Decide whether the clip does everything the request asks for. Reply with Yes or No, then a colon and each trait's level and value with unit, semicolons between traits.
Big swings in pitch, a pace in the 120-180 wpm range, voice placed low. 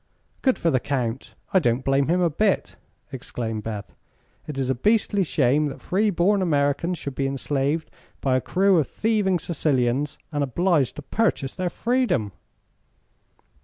No: wide, 5.7 semitones; average, 160 wpm; medium, 145 Hz